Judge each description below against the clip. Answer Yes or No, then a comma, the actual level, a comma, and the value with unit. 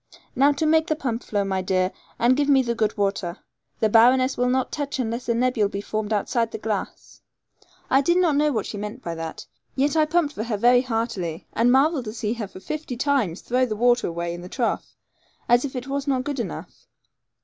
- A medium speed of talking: No, fast, 225 wpm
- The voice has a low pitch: No, high, 240 Hz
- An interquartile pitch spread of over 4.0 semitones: Yes, average, 4.6 semitones